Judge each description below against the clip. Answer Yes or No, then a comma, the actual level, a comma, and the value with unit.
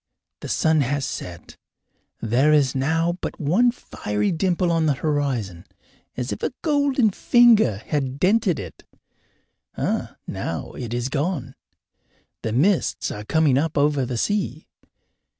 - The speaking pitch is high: No, medium, 150 Hz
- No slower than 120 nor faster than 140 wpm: Yes, slow, 135 wpm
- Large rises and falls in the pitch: Yes, wide, 6.2 semitones